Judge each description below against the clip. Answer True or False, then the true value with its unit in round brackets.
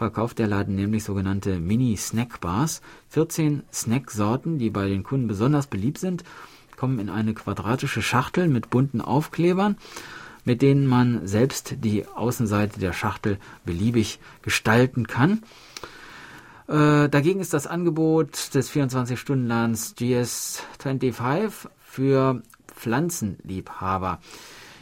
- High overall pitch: False (125 Hz)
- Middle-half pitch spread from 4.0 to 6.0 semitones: True (4.9 semitones)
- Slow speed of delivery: True (110 wpm)